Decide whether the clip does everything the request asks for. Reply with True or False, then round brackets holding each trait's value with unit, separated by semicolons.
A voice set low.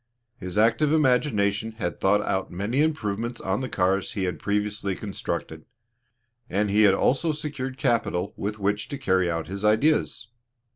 True (105 Hz)